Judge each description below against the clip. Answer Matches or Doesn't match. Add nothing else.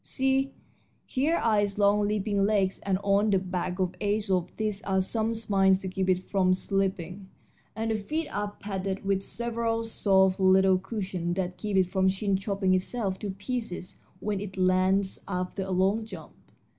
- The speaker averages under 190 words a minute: Matches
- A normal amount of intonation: Doesn't match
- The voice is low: Doesn't match